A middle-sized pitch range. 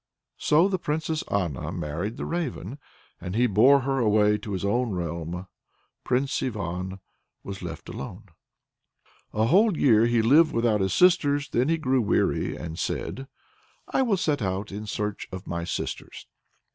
No: wide, 6.9 semitones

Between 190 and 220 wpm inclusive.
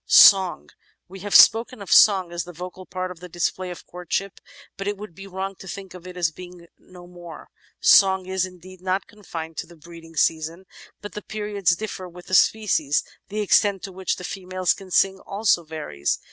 Yes: average, 200 wpm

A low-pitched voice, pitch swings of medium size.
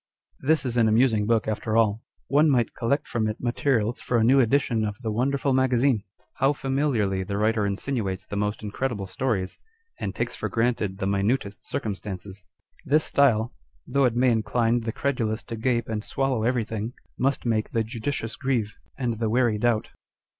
Yes: low, 115 Hz; average, 3.4 semitones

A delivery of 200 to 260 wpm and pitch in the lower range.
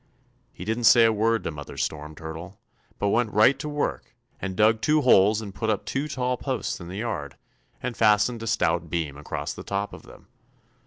Yes: fast, 205 wpm; low, 105 Hz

